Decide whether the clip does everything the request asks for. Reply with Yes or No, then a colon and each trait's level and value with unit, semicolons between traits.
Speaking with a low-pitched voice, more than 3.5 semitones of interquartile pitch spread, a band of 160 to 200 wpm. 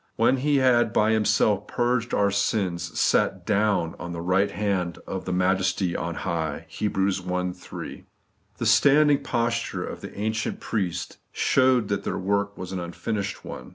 Yes: low, 100 Hz; average, 3.9 semitones; average, 165 wpm